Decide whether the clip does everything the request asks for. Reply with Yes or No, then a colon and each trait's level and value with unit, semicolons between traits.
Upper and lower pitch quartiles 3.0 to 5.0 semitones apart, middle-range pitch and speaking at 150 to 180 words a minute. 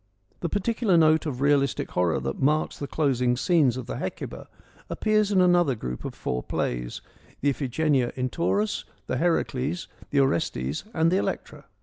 No: wide, 5.6 semitones; medium, 145 Hz; average, 160 wpm